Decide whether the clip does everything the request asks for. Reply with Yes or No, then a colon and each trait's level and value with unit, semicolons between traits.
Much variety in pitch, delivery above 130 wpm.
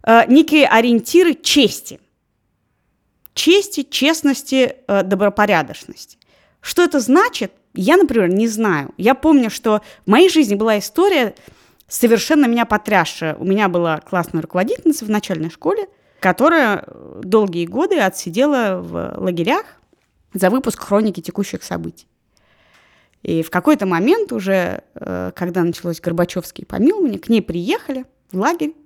No: wide, 7.4 semitones; average, 120 wpm